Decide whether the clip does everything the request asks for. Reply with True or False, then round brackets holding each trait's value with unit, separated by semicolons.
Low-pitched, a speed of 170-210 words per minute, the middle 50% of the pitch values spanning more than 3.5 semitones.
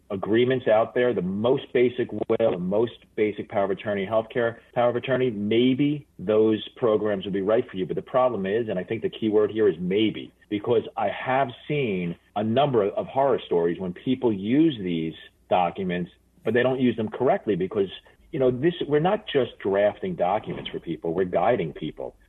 True (110 Hz; 195 wpm; 4.2 semitones)